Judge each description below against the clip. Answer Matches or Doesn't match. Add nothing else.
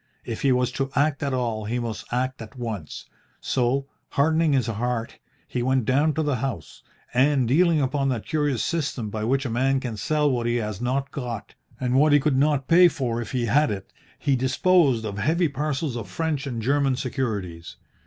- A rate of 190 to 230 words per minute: Matches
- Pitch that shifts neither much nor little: Matches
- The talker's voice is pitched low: Matches